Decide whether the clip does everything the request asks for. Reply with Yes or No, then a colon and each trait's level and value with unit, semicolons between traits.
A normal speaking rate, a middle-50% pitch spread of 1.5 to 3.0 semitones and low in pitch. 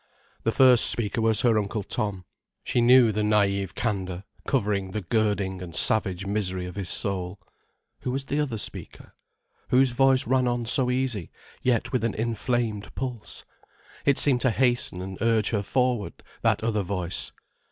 No: average, 165 wpm; average, 4.0 semitones; low, 110 Hz